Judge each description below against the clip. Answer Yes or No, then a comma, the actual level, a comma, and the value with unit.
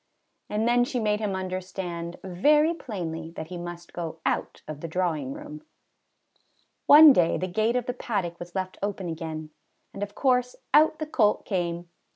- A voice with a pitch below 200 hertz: Yes, high, 190 Hz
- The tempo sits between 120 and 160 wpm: No, average, 175 wpm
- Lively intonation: Yes, wide, 6.0 semitones